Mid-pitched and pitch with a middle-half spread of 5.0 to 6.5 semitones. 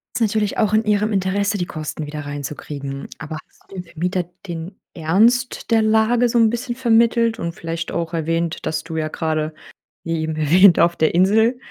Yes: medium, 180 Hz; wide, 5.5 semitones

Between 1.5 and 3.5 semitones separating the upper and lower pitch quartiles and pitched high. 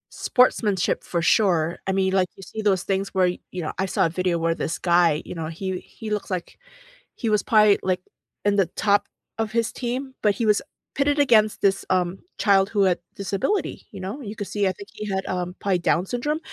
Yes: average, 2.8 semitones; high, 195 Hz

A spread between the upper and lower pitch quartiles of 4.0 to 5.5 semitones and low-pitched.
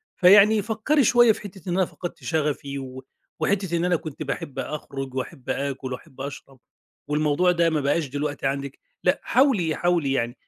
No: average, 4.8 semitones; medium, 155 Hz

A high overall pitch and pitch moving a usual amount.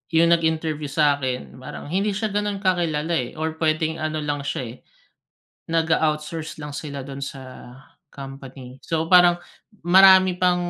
No: medium, 155 Hz; average, 3.6 semitones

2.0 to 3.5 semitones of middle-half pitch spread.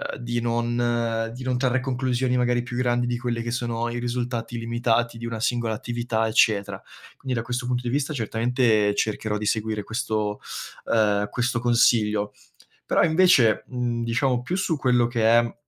No: narrow, 1.5 semitones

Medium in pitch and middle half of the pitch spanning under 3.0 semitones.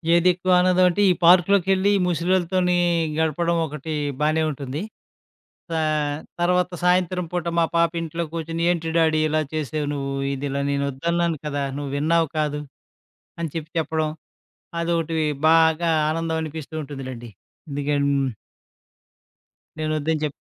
Yes: medium, 160 Hz; narrow, 2.4 semitones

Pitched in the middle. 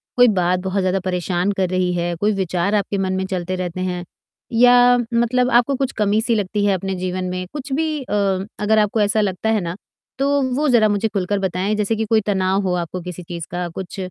No: high, 195 Hz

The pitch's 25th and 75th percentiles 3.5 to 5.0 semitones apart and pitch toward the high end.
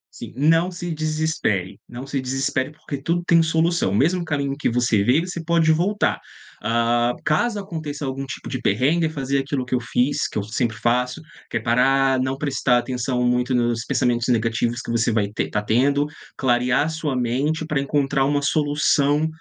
No: average, 4.1 semitones; low, 135 Hz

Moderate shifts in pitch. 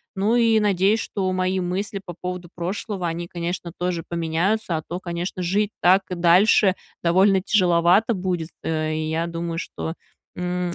No: narrow, 2.2 semitones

